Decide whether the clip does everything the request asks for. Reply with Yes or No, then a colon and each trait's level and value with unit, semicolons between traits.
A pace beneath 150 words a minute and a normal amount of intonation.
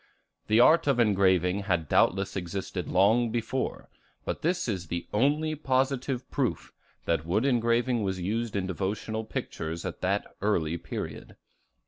Yes: average, 140 wpm; average, 4.8 semitones